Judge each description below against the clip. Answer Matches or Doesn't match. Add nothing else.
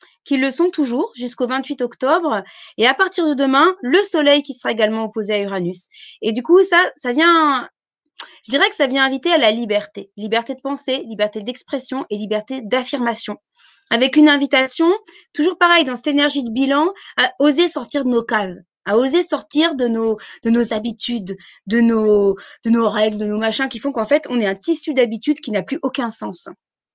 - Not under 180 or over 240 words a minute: Matches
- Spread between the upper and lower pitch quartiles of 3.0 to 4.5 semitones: Doesn't match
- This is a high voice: Matches